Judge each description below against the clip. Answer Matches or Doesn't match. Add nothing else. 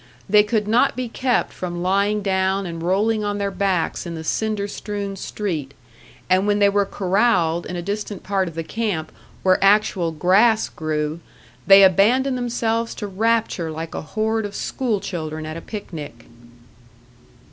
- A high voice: Matches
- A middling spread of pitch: Matches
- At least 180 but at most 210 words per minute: Doesn't match